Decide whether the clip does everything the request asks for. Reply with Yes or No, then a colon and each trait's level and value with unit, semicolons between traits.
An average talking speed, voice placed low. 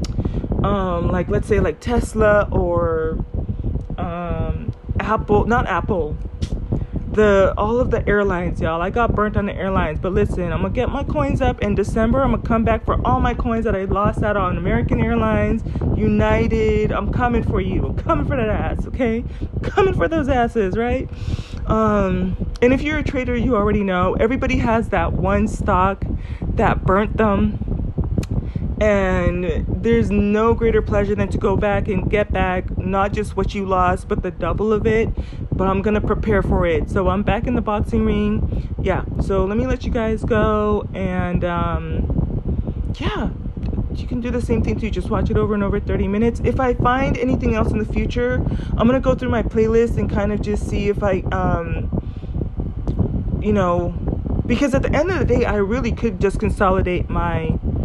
No: average, 190 wpm; medium, 185 Hz